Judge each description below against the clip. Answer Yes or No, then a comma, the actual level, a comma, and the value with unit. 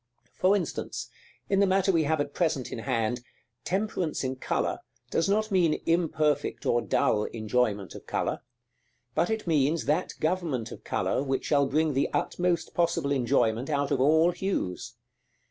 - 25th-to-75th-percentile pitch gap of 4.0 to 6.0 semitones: Yes, average, 5.3 semitones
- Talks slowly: No, average, 160 wpm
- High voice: No, medium, 150 Hz